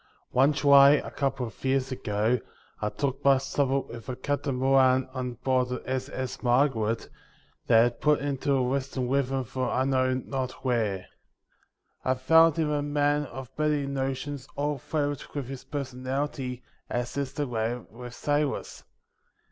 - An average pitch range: No, narrow, 2.0 semitones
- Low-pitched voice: Yes, low, 130 Hz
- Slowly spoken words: No, average, 155 wpm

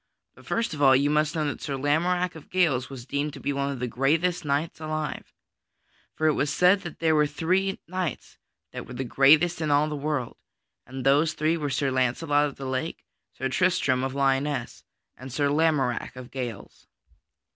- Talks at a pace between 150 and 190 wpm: No, average, 200 wpm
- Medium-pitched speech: Yes, medium, 145 Hz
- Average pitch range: Yes, average, 3.1 semitones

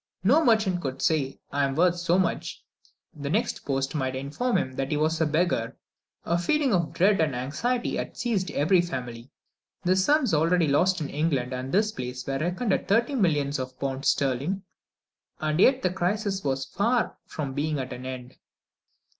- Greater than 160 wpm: Yes, average, 180 wpm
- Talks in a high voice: No, medium, 155 Hz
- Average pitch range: No, wide, 5.9 semitones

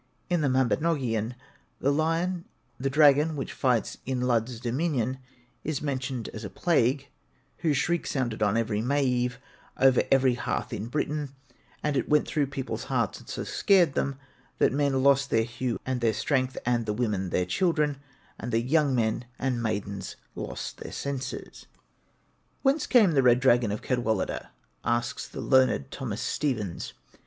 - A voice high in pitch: No, low, 130 Hz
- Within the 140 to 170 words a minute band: Yes, average, 160 wpm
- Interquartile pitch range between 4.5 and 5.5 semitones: No, average, 3.4 semitones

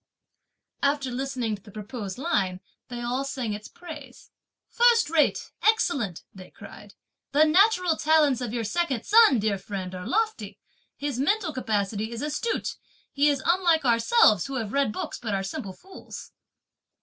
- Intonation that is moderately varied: No, wide, 6.9 semitones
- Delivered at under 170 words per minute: Yes, average, 155 wpm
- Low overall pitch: No, very high, 265 Hz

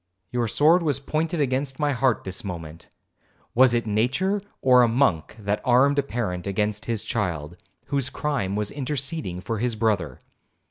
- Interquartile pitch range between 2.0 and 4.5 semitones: No, average, 5.3 semitones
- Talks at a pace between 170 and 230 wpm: No, average, 155 wpm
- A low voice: Yes, low, 120 Hz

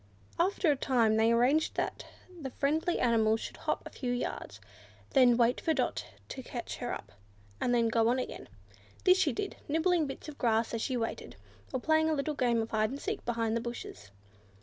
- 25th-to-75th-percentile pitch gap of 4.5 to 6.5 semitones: Yes, average, 5.0 semitones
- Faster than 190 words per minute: Yes, average, 200 wpm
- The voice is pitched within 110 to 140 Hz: No, very high, 250 Hz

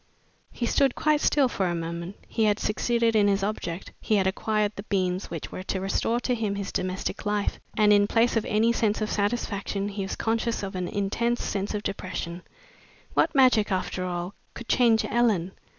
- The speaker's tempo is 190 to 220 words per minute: Yes, average, 195 wpm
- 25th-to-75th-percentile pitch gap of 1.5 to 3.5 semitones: Yes, average, 3.0 semitones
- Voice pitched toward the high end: Yes, high, 205 Hz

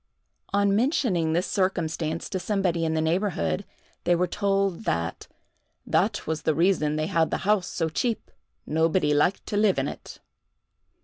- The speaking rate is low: No, average, 160 wpm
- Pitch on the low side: No, medium, 175 Hz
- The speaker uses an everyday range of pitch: Yes, average, 3.7 semitones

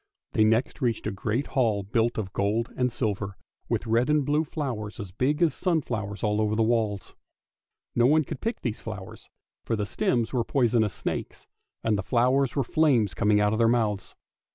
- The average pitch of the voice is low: Yes, low, 115 Hz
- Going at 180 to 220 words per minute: Yes, average, 190 wpm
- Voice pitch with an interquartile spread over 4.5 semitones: No, average, 3.7 semitones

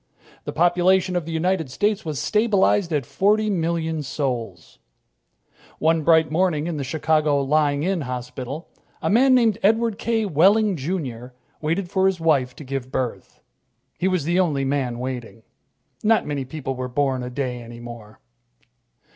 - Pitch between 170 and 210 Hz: No, medium, 155 Hz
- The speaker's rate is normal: Yes, average, 155 wpm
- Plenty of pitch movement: Yes, wide, 6.1 semitones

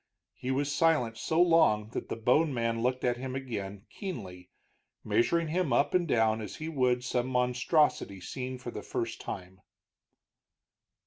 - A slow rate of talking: No, average, 155 wpm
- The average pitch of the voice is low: Yes, low, 125 Hz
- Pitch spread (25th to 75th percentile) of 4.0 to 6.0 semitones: Yes, average, 4.6 semitones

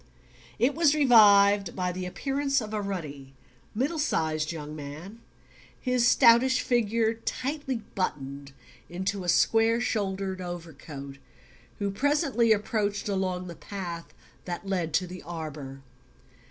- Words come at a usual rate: No, slow, 125 wpm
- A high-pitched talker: Yes, high, 195 Hz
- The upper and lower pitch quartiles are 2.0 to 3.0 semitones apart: No, wide, 5.5 semitones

